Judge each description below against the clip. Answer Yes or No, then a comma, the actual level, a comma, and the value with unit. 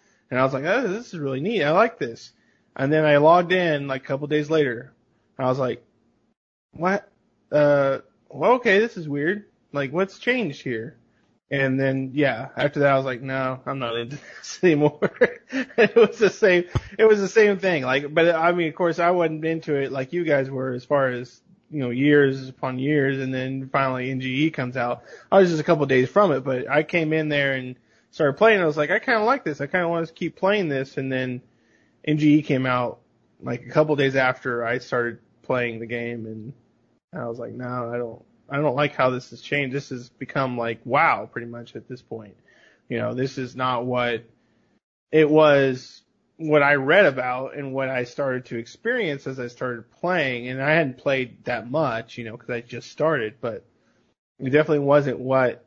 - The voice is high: No, low, 135 Hz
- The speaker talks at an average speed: No, fast, 215 wpm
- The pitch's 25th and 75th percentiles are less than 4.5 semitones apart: Yes, average, 3.6 semitones